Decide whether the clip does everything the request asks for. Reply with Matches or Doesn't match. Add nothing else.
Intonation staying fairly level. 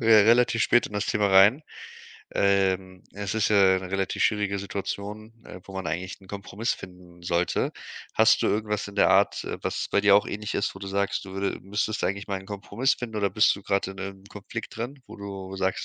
Matches